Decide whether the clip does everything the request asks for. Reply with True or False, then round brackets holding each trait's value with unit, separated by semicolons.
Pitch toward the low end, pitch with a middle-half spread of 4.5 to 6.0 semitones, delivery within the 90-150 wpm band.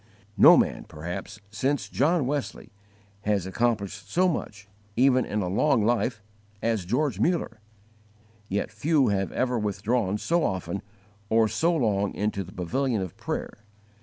True (110 Hz; 4.8 semitones; 140 wpm)